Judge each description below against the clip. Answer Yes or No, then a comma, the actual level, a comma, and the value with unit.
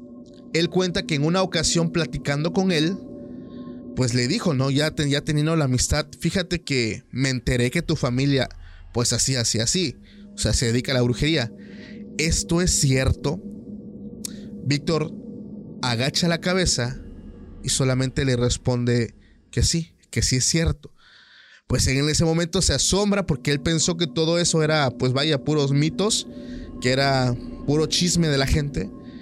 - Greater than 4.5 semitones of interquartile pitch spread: Yes, wide, 5.6 semitones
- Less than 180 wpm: Yes, average, 160 wpm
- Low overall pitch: No, medium, 150 Hz